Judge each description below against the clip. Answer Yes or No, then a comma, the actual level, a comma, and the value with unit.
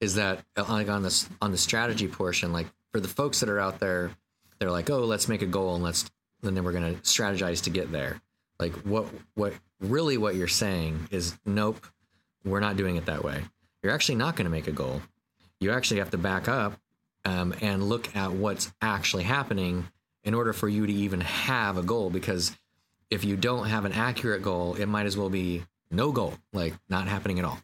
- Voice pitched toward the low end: Yes, very low, 95 Hz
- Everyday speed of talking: No, fast, 215 wpm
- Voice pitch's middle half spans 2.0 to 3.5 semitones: Yes, average, 2.9 semitones